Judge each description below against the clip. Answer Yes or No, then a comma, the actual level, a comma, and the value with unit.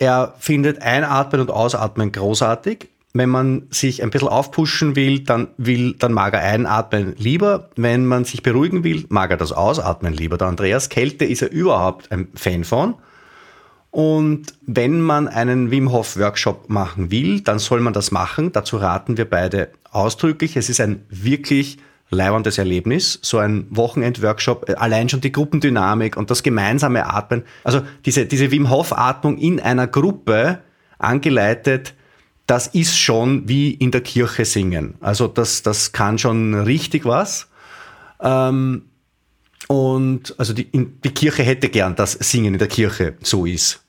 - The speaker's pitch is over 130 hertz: No, low, 125 Hz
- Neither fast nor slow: Yes, average, 155 wpm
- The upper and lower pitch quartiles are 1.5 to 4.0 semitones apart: No, average, 4.7 semitones